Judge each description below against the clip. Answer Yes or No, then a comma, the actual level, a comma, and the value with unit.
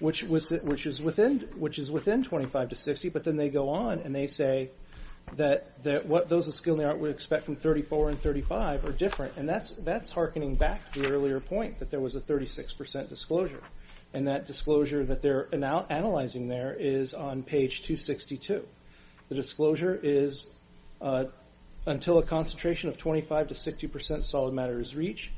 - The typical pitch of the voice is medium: Yes, medium, 145 Hz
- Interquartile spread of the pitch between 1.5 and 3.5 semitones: Yes, average, 2.7 semitones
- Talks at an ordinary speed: Yes, average, 180 wpm